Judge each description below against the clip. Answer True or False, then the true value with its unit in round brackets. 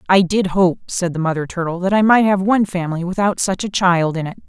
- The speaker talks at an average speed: False (255 wpm)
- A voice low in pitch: False (185 Hz)